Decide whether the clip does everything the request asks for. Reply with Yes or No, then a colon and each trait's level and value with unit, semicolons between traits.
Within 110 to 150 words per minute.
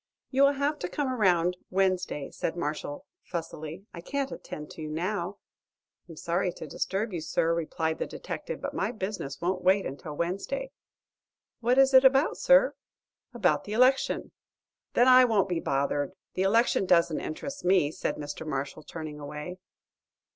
No: average, 160 wpm